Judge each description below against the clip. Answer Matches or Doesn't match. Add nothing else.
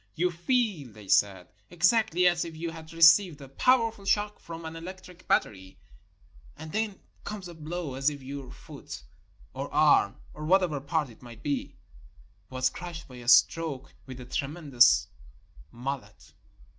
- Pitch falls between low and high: Matches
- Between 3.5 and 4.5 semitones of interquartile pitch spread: Doesn't match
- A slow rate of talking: Doesn't match